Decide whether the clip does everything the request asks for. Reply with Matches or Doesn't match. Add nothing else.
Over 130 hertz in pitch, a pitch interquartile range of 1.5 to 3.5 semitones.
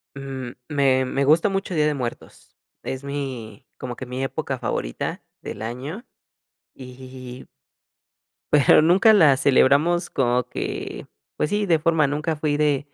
Matches